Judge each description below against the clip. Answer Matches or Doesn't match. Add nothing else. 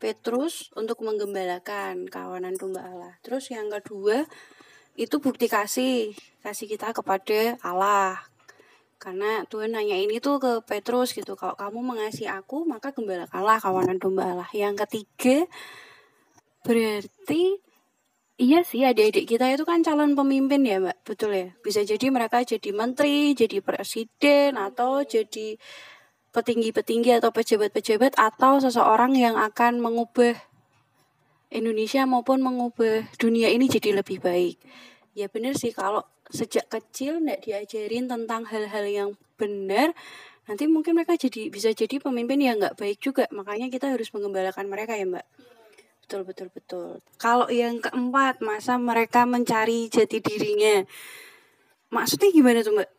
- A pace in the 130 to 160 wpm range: Matches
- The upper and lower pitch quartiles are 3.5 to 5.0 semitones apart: Matches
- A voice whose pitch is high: Matches